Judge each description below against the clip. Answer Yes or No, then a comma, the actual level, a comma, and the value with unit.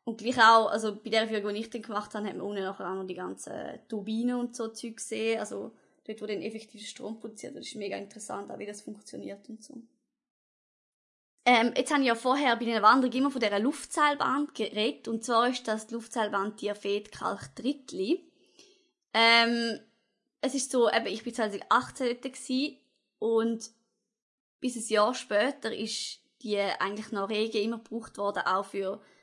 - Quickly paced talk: No, average, 180 wpm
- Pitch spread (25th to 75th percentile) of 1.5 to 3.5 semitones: Yes, average, 2.8 semitones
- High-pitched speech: Yes, high, 225 Hz